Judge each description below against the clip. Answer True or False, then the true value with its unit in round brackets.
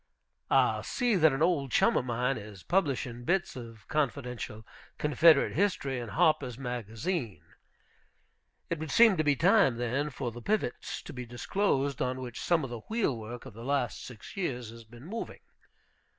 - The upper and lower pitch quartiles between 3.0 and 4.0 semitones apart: False (5.0 semitones)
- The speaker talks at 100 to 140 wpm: False (165 wpm)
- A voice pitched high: False (130 Hz)